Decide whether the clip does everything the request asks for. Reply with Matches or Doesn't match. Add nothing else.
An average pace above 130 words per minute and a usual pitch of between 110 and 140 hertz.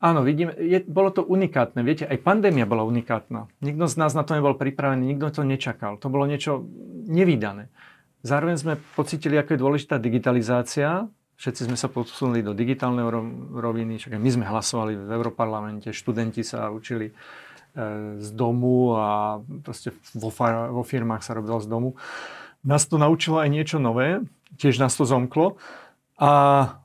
Matches